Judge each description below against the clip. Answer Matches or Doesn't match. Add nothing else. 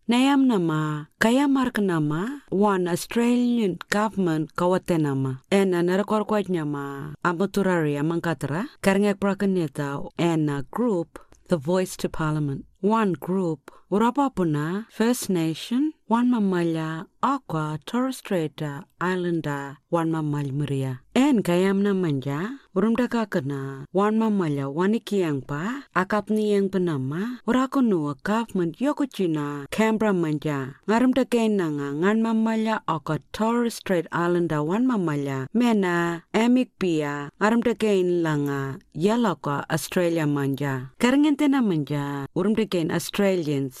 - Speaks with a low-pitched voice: Doesn't match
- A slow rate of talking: Matches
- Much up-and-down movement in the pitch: Matches